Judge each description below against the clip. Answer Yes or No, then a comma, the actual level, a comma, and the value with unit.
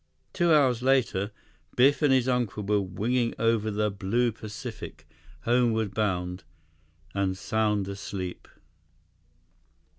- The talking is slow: Yes, slow, 100 wpm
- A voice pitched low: Yes, low, 105 Hz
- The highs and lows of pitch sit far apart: No, average, 4.3 semitones